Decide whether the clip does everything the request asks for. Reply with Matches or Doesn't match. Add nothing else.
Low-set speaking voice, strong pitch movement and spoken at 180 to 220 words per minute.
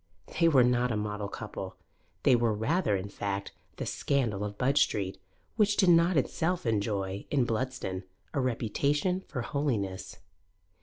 Doesn't match